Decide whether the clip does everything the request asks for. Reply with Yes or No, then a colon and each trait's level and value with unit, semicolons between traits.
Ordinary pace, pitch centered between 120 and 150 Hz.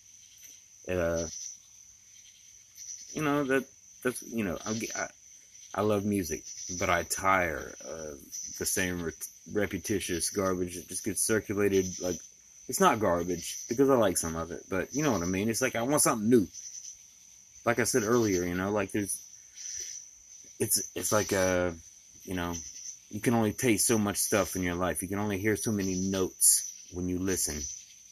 No: average, 175 wpm; very low, 95 Hz